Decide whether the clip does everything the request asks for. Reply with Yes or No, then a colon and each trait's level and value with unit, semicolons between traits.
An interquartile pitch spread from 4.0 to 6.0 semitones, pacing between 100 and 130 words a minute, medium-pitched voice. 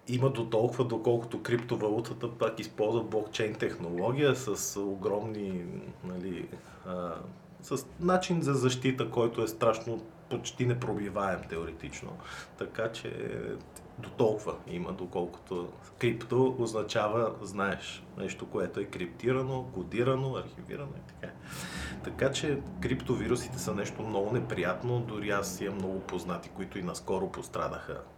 No: average, 4.4 semitones; average, 120 wpm; low, 115 Hz